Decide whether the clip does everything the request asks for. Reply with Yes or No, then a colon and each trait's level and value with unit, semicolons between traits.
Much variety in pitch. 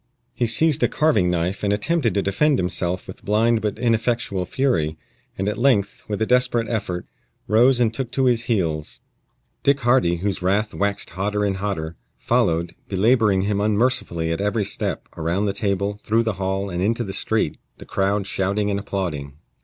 No: average, 3.5 semitones